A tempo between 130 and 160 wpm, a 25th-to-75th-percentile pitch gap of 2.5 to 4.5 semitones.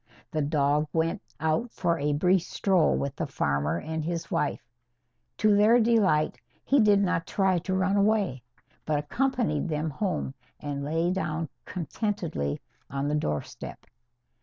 No: average, 145 wpm; average, 4.9 semitones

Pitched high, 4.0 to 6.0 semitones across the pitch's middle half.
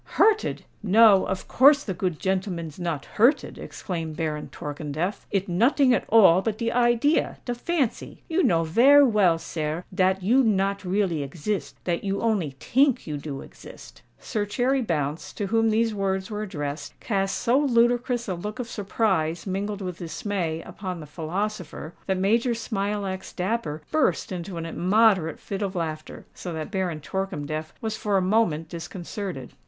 Yes: high, 195 Hz; average, 5.1 semitones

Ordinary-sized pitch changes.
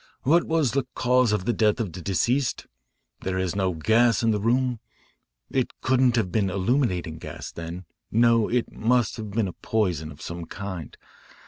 Yes: average, 4.9 semitones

